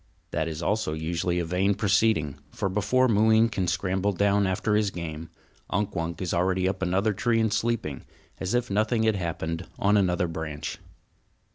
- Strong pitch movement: No, average, 3.8 semitones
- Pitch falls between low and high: No, very low, 95 Hz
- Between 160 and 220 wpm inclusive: Yes, average, 170 wpm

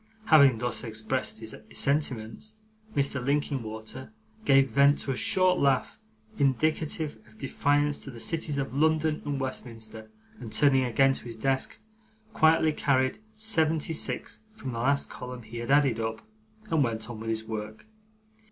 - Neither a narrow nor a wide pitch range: Yes, average, 4.3 semitones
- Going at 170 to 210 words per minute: No, average, 150 wpm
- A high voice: No, low, 135 Hz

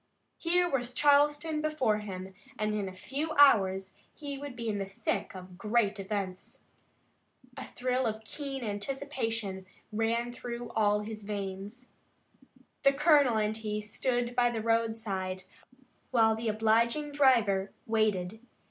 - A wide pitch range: No, average, 4.2 semitones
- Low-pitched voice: No, high, 225 Hz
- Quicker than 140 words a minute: No, slow, 135 wpm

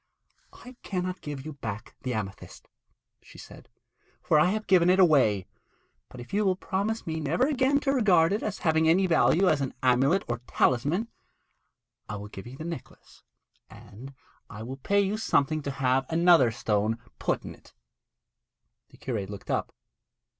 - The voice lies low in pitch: No, medium, 155 Hz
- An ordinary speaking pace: Yes, average, 170 wpm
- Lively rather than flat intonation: Yes, wide, 7.1 semitones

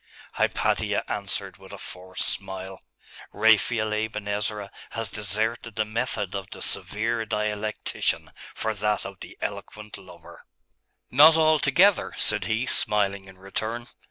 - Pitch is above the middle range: No, low, 105 Hz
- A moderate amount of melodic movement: No, narrow, 2.2 semitones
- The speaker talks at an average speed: No, slow, 130 wpm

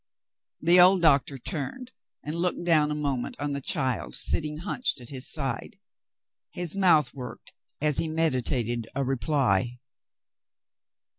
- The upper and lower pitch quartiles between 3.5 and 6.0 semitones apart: Yes, average, 4.3 semitones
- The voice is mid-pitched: Yes, medium, 145 Hz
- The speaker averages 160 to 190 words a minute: No, slow, 135 wpm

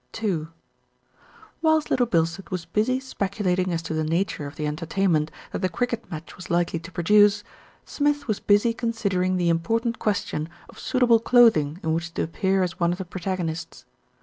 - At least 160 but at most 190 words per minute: Yes, average, 175 wpm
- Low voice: No, medium, 185 Hz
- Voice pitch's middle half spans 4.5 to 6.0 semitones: Yes, average, 5.0 semitones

